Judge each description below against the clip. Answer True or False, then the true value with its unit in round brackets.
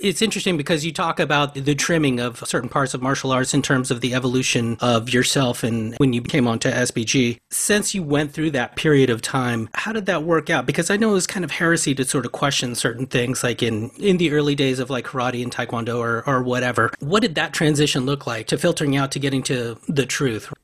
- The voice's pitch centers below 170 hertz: True (135 Hz)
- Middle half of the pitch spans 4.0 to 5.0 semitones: True (4.3 semitones)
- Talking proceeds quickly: True (240 wpm)